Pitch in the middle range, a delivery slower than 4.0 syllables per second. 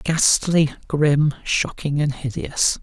Yes: medium, 150 Hz; 3.2 syllables/s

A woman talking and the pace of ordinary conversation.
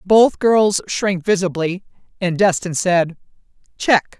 No: female; slow, 115 wpm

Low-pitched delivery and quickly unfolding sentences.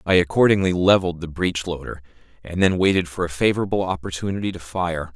No: very low, 90 Hz; average, 175 wpm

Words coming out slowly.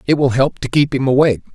No: fast, 270 wpm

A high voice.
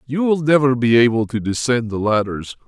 No: low, 125 Hz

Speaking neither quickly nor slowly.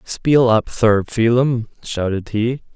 No: slow, 130 wpm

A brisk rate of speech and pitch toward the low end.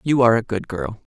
Yes: fast, 270 wpm; low, 130 Hz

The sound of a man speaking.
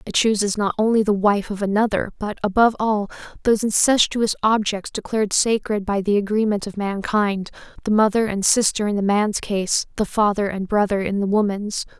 No: female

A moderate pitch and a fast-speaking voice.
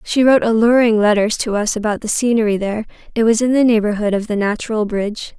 No: high, 220 Hz; fast, 210 wpm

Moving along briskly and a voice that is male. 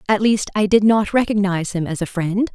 No: fast, 235 wpm; female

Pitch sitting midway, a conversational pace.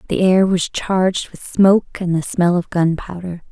Yes: medium, 180 Hz; average, 190 wpm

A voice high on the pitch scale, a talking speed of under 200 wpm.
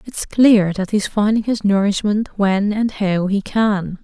Yes: high, 205 Hz; average, 180 wpm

